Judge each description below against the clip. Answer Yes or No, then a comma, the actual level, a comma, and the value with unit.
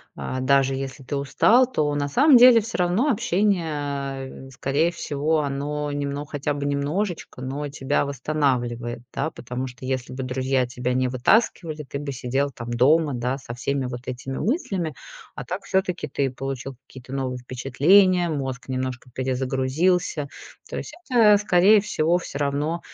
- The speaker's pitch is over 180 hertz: No, medium, 140 Hz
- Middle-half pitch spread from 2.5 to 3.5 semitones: No, average, 4.5 semitones